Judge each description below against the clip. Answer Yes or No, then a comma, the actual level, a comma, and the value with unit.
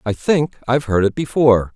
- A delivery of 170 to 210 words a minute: Yes, fast, 205 wpm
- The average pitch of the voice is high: No, low, 125 Hz